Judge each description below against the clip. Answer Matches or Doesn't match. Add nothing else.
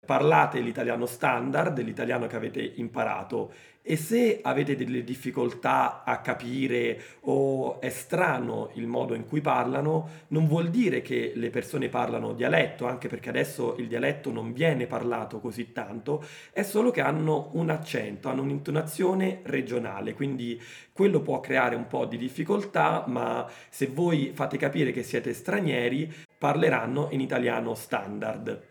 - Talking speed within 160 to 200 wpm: Doesn't match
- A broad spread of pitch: Doesn't match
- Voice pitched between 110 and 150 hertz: Matches